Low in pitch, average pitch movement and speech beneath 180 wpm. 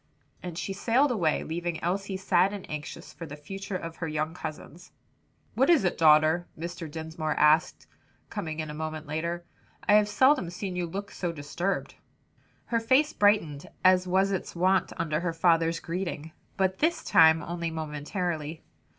No: medium, 170 Hz; average, 3.4 semitones; average, 165 wpm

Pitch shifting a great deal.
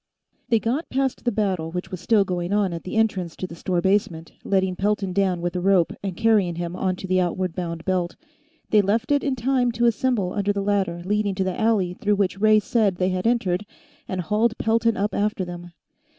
No: average, 3.2 semitones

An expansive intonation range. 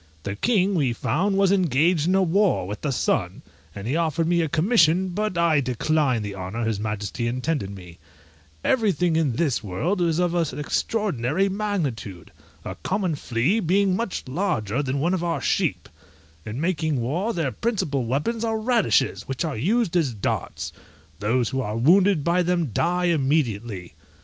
Yes: wide, 7.3 semitones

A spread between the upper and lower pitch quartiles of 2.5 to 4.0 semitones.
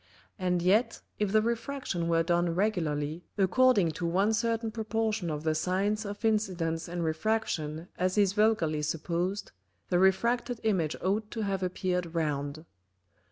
No: average, 4.6 semitones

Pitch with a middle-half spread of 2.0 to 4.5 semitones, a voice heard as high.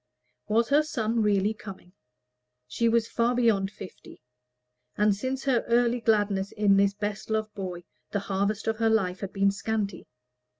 Yes: narrow, 2.6 semitones; high, 210 Hz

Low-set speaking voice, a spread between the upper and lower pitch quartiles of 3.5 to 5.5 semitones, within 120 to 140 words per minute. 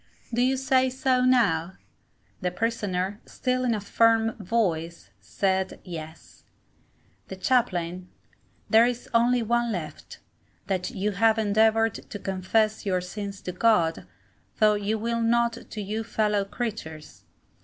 No: high, 215 Hz; average, 3.9 semitones; slow, 135 wpm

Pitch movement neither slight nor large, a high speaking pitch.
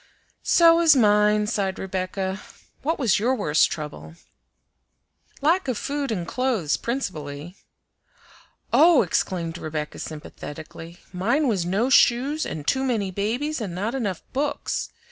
No: wide, 7.2 semitones; high, 210 Hz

